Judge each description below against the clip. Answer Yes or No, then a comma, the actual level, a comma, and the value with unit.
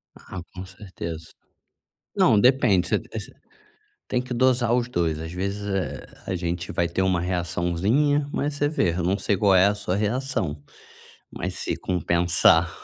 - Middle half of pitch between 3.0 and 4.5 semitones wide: No, wide, 5.4 semitones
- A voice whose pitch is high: No, very low, 95 Hz